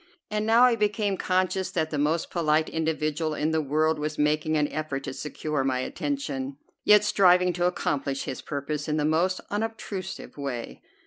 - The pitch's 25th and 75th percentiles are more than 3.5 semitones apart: Yes, average, 3.9 semitones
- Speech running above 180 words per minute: No, average, 175 wpm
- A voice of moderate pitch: Yes, medium, 155 Hz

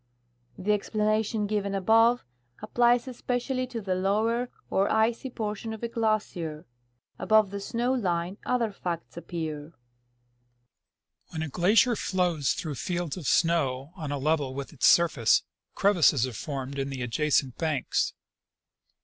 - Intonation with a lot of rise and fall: Yes, wide, 6.2 semitones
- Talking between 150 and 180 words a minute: No, slow, 135 wpm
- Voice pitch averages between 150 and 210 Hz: Yes, medium, 185 Hz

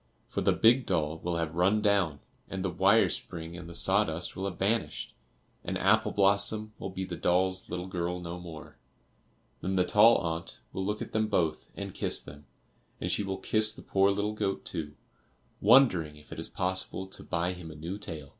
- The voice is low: Yes, very low, 95 Hz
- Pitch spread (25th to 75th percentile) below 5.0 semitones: Yes, average, 3.3 semitones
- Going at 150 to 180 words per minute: No, average, 200 wpm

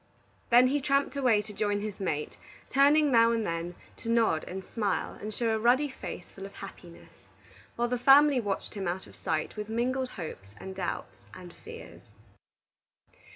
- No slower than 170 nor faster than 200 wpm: Yes, average, 175 wpm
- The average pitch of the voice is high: Yes, high, 220 Hz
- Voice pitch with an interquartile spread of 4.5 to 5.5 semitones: Yes, average, 5.0 semitones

